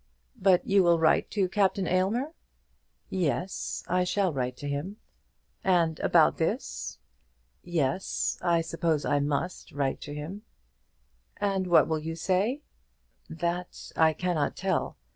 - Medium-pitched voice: Yes, medium, 175 Hz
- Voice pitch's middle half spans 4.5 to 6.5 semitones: No, average, 3.4 semitones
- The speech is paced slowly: Yes, slow, 130 wpm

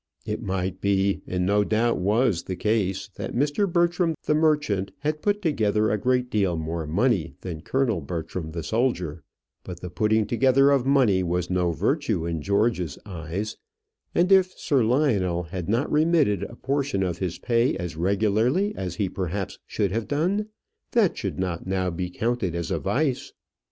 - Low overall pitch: Yes, low, 105 Hz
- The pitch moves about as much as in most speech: No, wide, 6.7 semitones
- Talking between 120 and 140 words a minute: No, average, 170 wpm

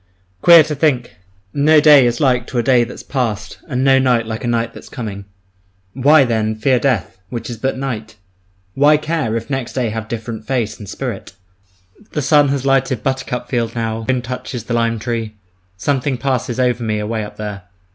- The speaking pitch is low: Yes, low, 120 Hz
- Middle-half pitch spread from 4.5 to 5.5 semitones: No, average, 3.1 semitones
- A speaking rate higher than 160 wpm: Yes, average, 195 wpm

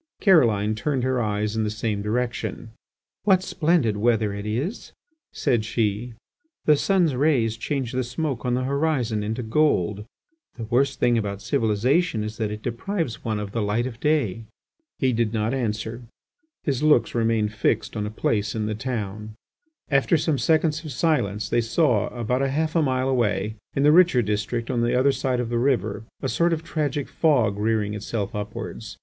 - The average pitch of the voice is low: Yes, low, 120 Hz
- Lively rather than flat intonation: No, average, 4.6 semitones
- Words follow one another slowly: No, average, 180 wpm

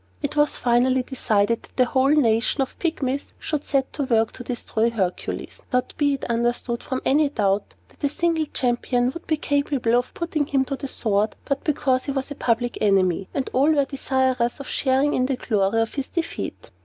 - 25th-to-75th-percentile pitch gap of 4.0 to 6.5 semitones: No, average, 3.2 semitones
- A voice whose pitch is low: No, very high, 260 Hz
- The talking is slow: No, average, 200 wpm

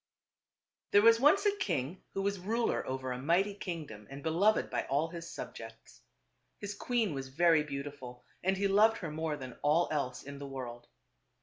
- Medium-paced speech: Yes, average, 180 wpm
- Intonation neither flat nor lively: No, wide, 6.7 semitones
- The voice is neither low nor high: Yes, medium, 160 Hz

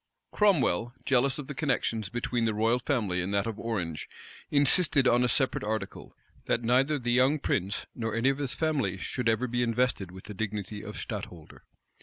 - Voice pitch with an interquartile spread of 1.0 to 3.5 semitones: No, average, 4.0 semitones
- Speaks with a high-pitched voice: No, low, 120 Hz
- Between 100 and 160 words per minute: No, average, 185 wpm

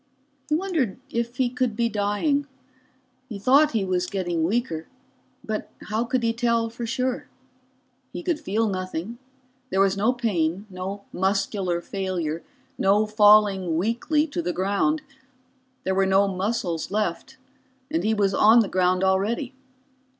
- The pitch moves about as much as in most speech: Yes, average, 3.8 semitones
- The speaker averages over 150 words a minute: No, average, 145 wpm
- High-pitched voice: Yes, high, 210 Hz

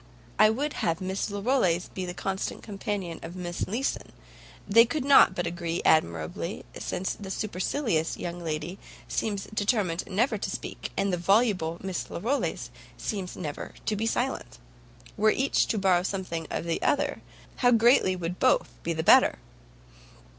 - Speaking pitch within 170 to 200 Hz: Yes, high, 190 Hz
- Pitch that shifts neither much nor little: Yes, average, 4.3 semitones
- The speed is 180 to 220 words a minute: No, average, 155 wpm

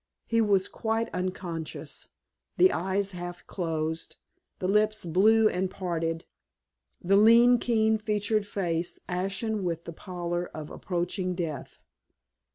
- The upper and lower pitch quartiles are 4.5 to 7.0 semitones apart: No, average, 3.6 semitones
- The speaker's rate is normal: No, slow, 120 wpm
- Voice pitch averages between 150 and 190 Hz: Yes, medium, 185 Hz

